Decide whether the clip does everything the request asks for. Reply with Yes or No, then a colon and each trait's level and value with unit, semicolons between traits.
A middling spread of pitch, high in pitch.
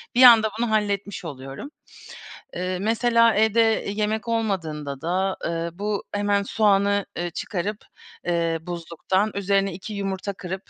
Yes: average, 3.5 semitones; high, 200 Hz